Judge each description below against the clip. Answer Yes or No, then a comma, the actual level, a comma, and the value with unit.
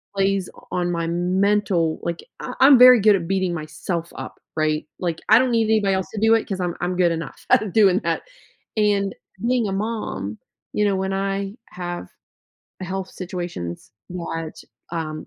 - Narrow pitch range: No, average, 3.3 semitones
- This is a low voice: No, high, 190 Hz